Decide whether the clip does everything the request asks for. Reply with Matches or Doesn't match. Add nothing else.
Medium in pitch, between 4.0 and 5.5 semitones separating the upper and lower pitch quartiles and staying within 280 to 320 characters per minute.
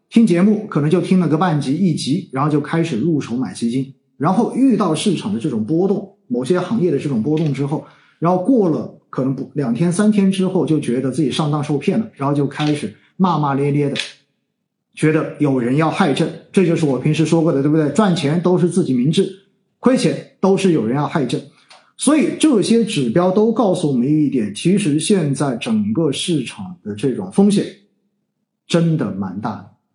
Matches